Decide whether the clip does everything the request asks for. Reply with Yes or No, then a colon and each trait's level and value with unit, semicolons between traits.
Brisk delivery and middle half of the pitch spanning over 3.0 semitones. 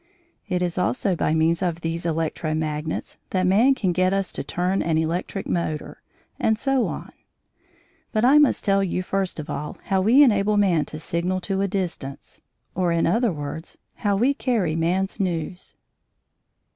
No: average, 170 wpm; average, 3.4 semitones